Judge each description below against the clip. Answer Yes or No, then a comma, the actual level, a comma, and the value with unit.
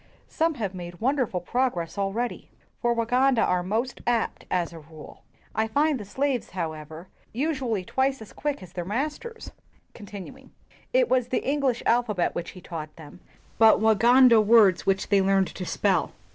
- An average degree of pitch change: No, wide, 6.0 semitones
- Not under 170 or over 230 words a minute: No, average, 160 wpm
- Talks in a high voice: Yes, high, 220 Hz